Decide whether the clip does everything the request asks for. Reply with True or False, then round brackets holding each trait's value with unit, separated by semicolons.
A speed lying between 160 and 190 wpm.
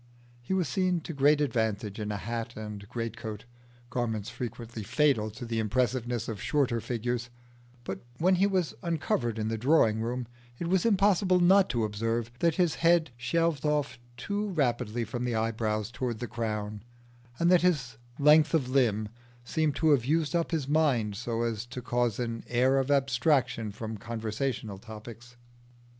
True (165 wpm)